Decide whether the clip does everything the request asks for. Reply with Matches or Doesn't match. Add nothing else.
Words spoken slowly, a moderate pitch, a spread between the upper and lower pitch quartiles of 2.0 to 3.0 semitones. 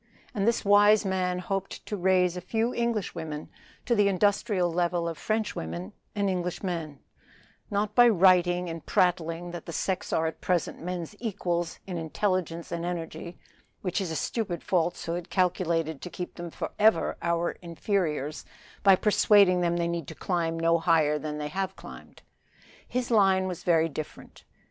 Doesn't match